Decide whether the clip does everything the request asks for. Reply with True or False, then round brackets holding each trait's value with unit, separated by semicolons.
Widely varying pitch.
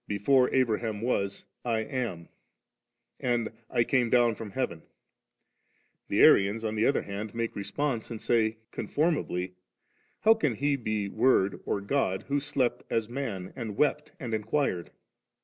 False (4.3 semitones)